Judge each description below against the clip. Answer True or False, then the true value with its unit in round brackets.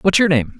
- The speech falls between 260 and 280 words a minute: False (300 wpm)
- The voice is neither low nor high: True (165 Hz)